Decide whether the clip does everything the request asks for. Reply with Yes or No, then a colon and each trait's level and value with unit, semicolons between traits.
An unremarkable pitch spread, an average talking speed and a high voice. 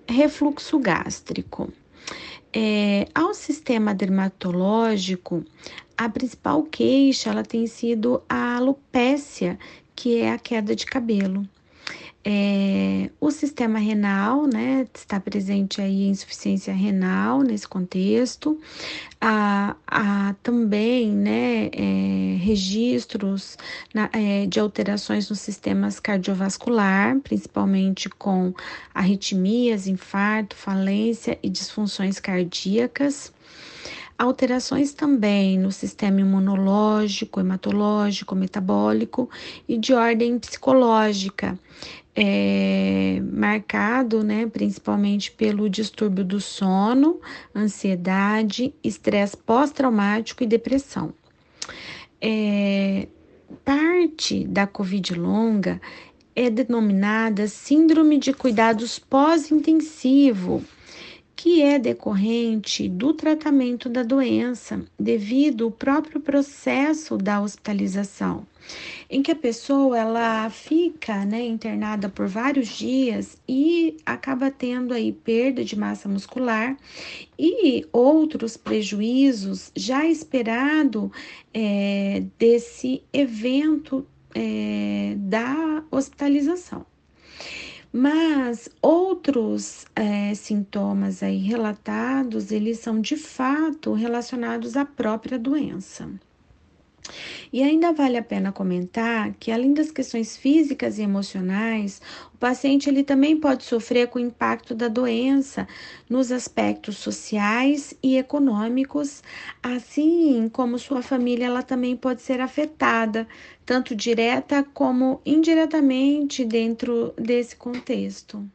No: average, 4.8 semitones; slow, 95 wpm; high, 230 Hz